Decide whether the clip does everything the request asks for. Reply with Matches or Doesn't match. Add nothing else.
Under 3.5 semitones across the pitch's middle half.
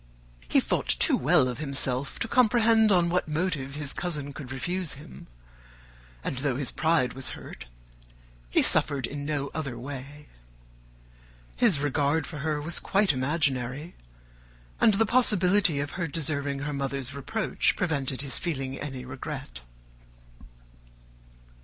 Doesn't match